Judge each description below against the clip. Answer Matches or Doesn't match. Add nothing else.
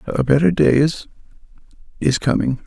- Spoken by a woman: Doesn't match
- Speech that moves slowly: Matches